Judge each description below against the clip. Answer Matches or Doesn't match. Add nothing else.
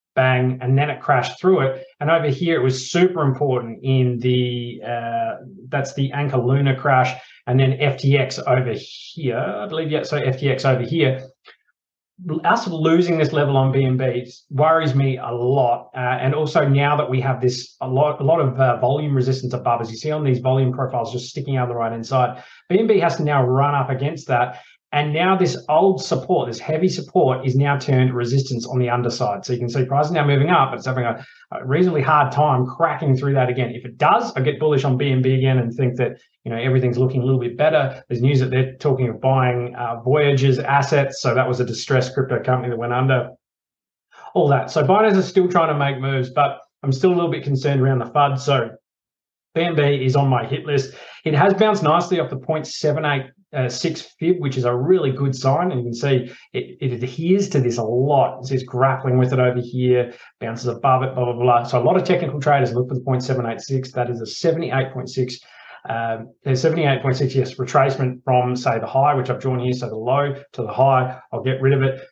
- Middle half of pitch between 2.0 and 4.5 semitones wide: Matches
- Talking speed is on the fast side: Matches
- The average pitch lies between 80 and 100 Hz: Doesn't match